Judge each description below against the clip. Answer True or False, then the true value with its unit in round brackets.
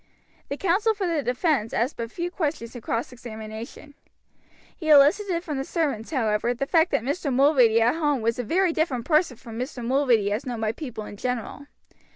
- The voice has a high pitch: True (265 Hz)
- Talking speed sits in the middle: True (190 wpm)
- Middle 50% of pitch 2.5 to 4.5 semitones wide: False (5.4 semitones)